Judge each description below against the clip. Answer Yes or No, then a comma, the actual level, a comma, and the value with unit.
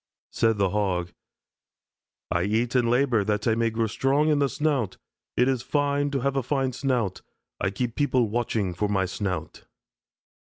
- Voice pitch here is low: Yes, low, 115 Hz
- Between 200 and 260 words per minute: No, average, 175 wpm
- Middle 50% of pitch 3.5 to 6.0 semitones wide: Yes, average, 4.7 semitones